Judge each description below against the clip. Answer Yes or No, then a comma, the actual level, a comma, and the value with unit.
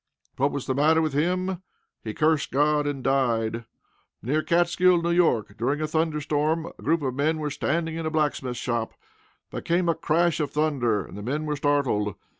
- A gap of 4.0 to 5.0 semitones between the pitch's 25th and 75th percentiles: No, average, 3.3 semitones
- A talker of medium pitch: Yes, medium, 150 Hz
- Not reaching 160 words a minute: No, average, 190 wpm